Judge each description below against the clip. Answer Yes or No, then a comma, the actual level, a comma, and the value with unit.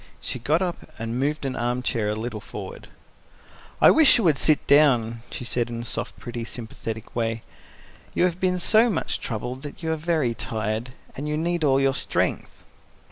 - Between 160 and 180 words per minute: No, average, 190 wpm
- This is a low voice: Yes, low, 130 Hz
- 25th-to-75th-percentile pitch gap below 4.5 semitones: No, wide, 5.6 semitones